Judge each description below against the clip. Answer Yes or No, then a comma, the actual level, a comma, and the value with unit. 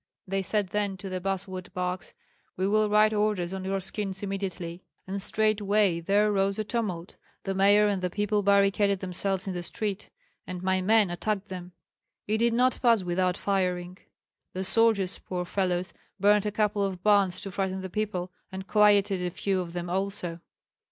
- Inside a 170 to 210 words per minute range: Yes, average, 180 wpm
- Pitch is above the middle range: Yes, high, 195 Hz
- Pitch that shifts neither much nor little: No, narrow, 2.2 semitones